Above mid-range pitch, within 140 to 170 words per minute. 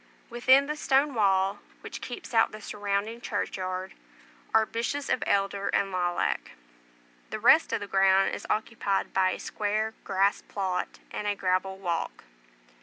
Yes: high, 200 Hz; average, 150 wpm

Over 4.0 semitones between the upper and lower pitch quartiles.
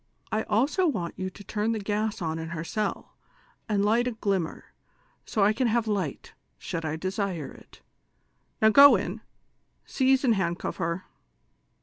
Yes: average, 4.5 semitones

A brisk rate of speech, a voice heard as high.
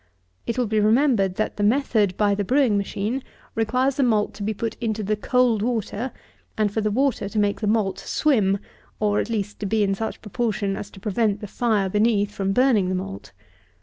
Yes: fast, 210 wpm; high, 215 Hz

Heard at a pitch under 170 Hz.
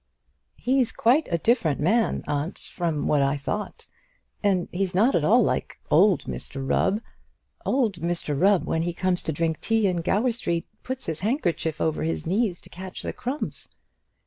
No: medium, 180 Hz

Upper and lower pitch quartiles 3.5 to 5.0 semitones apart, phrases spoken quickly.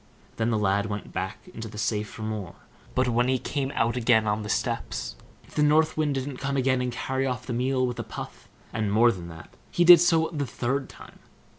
Yes: average, 3.9 semitones; fast, 230 wpm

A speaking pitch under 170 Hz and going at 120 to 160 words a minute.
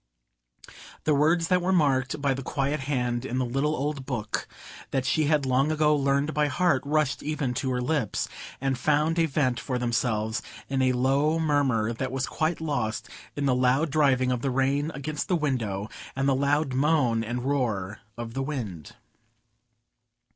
No: low, 135 Hz; average, 175 wpm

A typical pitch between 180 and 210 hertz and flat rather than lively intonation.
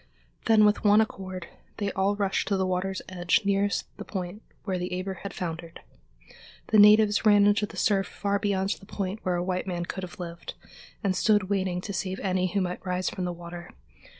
Yes: high, 190 Hz; narrow, 2.0 semitones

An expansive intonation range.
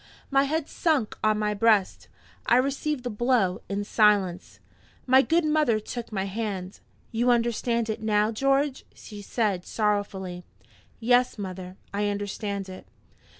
No: average, 3.7 semitones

